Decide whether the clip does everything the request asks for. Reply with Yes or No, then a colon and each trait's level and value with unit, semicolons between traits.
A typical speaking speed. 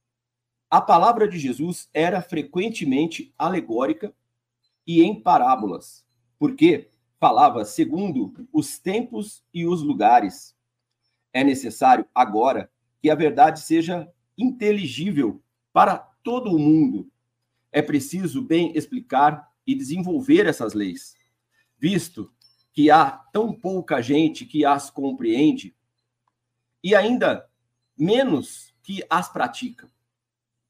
No: slow, 105 wpm